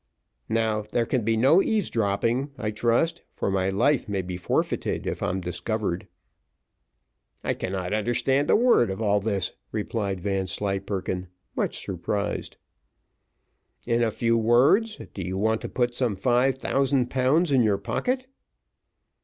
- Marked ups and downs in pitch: No, average, 4.6 semitones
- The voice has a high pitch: No, low, 110 Hz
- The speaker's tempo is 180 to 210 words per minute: No, average, 140 wpm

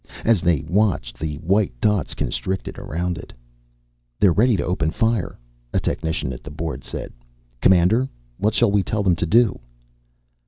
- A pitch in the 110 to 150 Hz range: No, very low, 95 Hz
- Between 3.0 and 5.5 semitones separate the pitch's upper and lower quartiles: Yes, average, 4.6 semitones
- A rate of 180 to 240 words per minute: No, average, 160 wpm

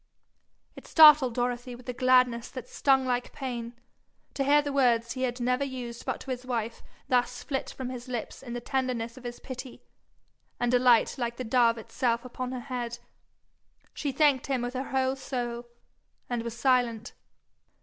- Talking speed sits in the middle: Yes, average, 170 wpm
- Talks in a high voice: Yes, very high, 250 Hz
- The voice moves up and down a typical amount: No, narrow, 1.5 semitones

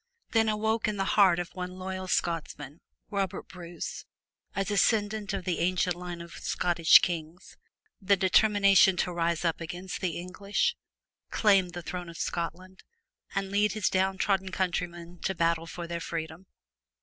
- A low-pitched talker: No, medium, 180 Hz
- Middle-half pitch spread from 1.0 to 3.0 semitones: Yes, narrow, 2.4 semitones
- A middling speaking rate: Yes, average, 155 wpm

